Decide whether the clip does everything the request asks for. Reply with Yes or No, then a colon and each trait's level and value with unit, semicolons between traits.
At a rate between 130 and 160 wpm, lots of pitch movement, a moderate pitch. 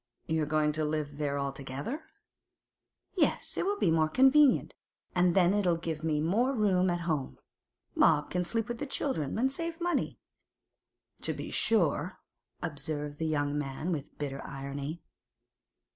Yes: average, 145 wpm; wide, 5.9 semitones; medium, 160 Hz